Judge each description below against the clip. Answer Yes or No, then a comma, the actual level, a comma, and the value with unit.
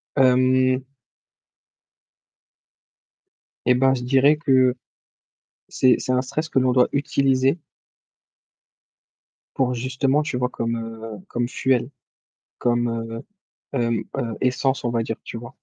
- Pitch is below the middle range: Yes, low, 130 Hz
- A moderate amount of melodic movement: No, narrow, 1.9 semitones